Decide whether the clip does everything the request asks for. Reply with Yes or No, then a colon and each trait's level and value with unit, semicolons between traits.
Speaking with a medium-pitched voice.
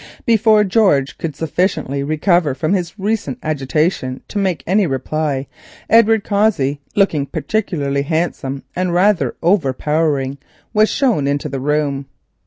Yes: medium, 160 Hz